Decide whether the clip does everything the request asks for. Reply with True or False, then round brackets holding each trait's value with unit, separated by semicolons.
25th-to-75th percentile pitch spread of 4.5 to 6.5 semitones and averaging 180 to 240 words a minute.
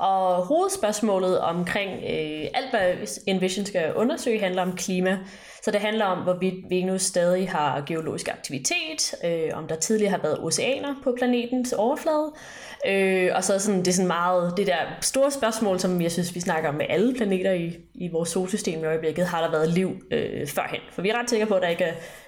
False (3.7 semitones; 205 wpm)